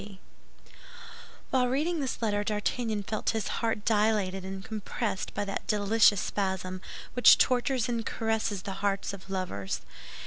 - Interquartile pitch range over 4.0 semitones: No, average, 2.8 semitones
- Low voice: No, high, 210 Hz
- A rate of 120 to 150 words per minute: Yes, average, 140 wpm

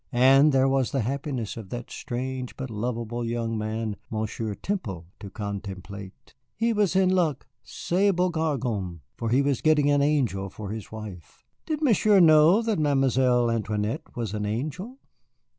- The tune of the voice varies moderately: No, wide, 5.9 semitones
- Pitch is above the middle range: No, low, 125 Hz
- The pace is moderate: Yes, average, 160 wpm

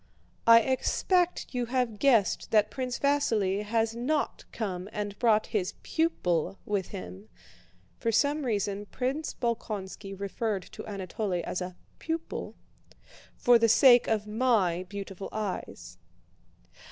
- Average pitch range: Yes, average, 4.1 semitones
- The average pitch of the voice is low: No, high, 215 Hz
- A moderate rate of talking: No, slow, 125 wpm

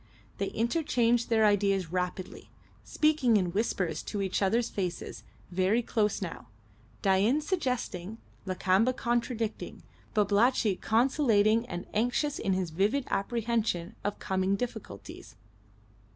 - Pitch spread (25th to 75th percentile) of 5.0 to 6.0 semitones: No, average, 3.9 semitones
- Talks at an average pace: No, slow, 110 wpm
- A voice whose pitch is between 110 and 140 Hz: No, high, 210 Hz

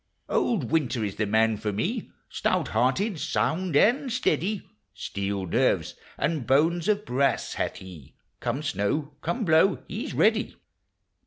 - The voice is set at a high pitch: No, medium, 150 Hz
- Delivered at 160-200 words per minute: No, average, 150 wpm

